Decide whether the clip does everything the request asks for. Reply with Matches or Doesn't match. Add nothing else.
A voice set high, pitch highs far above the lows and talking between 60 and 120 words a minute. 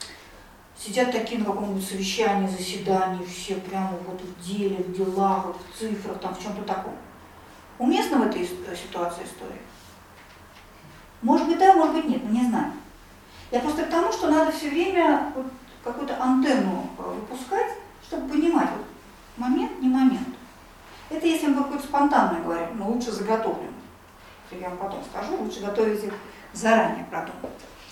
Doesn't match